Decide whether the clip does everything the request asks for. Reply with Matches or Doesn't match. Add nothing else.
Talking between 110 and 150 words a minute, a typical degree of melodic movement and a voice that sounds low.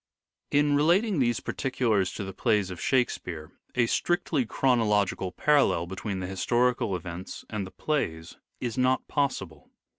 Doesn't match